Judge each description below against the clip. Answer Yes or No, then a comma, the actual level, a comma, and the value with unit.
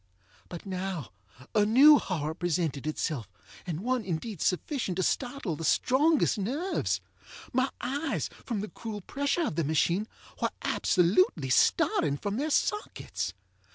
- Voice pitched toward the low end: No, high, 200 Hz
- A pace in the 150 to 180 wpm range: No, slow, 135 wpm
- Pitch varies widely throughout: Yes, wide, 7.7 semitones